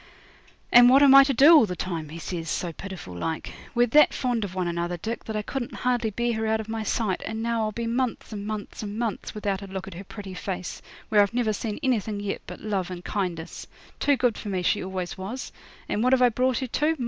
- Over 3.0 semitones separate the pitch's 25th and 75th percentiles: Yes, average, 4.2 semitones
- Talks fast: Yes, fast, 250 wpm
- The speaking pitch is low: No, high, 215 Hz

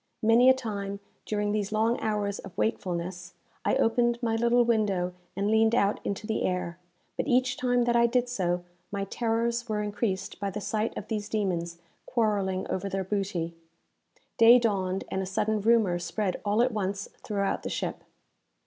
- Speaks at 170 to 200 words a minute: Yes, average, 175 wpm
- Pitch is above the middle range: Yes, high, 210 Hz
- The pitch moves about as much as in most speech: Yes, average, 3.3 semitones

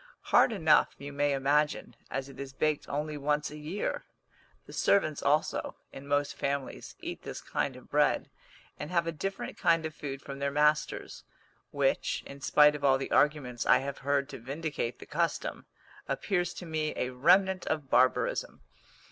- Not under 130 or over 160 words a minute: No, average, 175 wpm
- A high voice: No, medium, 150 Hz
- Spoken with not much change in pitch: Yes, narrow, 2.0 semitones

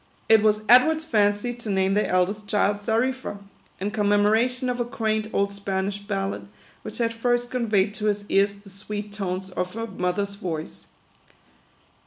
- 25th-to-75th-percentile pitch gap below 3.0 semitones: Yes, narrow, 2.4 semitones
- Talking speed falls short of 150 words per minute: No, average, 160 wpm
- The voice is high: Yes, high, 205 Hz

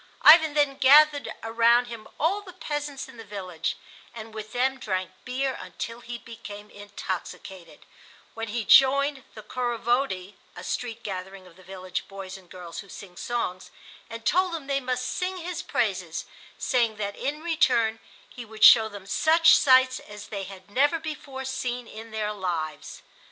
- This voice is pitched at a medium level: No, high, 230 Hz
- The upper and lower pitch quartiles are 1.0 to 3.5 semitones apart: No, average, 5.3 semitones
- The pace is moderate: Yes, average, 165 wpm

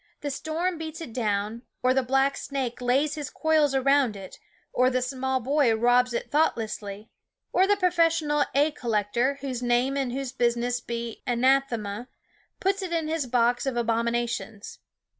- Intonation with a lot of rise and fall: No, average, 3.6 semitones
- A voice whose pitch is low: No, very high, 255 Hz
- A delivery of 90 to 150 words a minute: No, average, 165 wpm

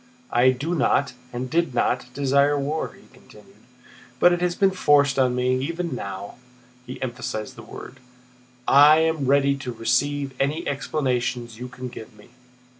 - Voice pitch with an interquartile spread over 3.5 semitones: No, average, 2.8 semitones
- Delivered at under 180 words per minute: Yes, average, 160 wpm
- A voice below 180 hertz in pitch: Yes, low, 135 Hz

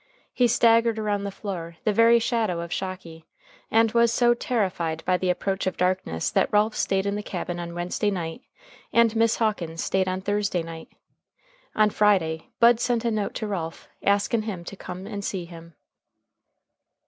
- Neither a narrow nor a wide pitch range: Yes, average, 4.2 semitones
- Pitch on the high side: Yes, high, 200 Hz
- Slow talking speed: No, average, 175 wpm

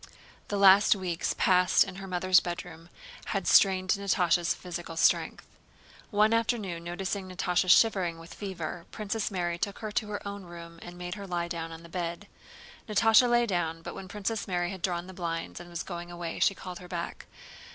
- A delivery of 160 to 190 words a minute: Yes, average, 185 wpm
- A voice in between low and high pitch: Yes, medium, 180 Hz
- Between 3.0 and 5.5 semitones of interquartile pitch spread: No, narrow, 2.5 semitones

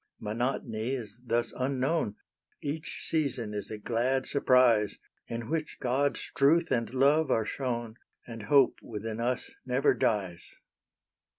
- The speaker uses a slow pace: Yes, slow, 125 wpm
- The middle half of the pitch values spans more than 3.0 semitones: Yes, average, 3.5 semitones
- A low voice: Yes, low, 125 Hz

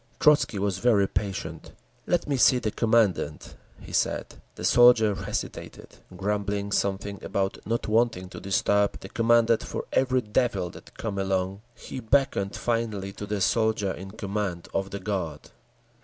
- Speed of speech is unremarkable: Yes, average, 150 wpm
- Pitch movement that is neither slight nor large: Yes, average, 3.0 semitones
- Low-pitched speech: Yes, low, 100 Hz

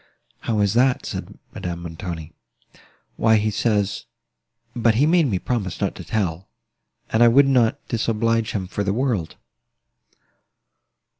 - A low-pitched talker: Yes, low, 110 Hz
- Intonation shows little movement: No, average, 3.8 semitones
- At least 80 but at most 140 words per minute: Yes, slow, 135 wpm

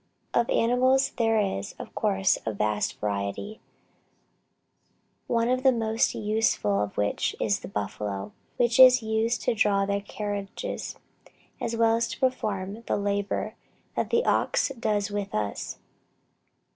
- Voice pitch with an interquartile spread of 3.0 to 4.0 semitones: Yes, average, 3.5 semitones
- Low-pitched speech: No, high, 215 Hz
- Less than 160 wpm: Yes, average, 140 wpm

